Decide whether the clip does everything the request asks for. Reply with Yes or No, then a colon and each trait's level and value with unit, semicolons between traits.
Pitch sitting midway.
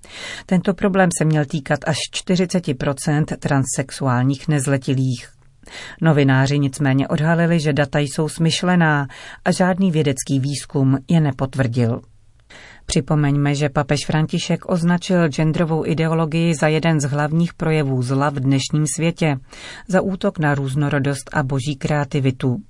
Yes: medium, 150 Hz